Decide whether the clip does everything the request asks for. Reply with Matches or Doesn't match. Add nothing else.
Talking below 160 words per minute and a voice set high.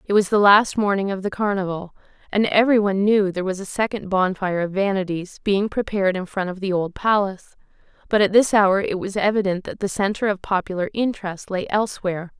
Doesn't match